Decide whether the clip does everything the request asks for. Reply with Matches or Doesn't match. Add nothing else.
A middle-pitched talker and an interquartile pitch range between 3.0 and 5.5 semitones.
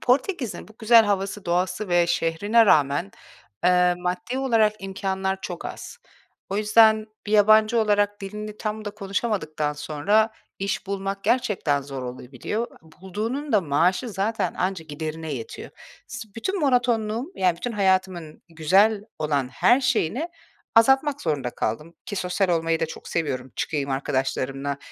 Doesn't match